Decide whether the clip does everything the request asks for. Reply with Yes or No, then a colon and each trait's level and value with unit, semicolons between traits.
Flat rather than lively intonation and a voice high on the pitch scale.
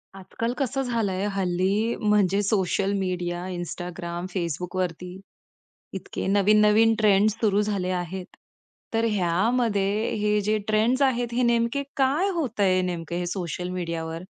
No: average, 3.8 semitones; high, 200 Hz